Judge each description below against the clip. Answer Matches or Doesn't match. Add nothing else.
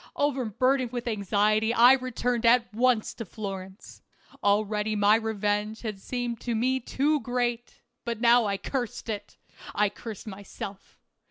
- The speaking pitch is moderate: Doesn't match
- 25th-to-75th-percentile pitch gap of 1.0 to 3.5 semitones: Matches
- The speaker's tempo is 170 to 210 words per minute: Doesn't match